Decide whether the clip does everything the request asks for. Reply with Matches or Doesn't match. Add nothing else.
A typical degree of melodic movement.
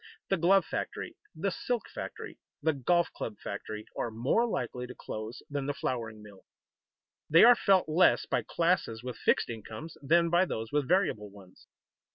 Doesn't match